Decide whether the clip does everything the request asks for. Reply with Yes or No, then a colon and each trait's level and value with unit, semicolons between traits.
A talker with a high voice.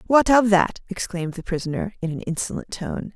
Yes: high, 195 Hz